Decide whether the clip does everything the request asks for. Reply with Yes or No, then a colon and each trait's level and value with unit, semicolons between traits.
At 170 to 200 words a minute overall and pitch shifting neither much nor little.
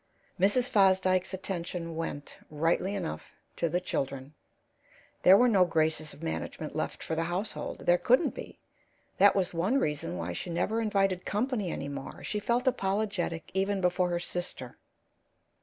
No: average, 155 wpm; average, 3.6 semitones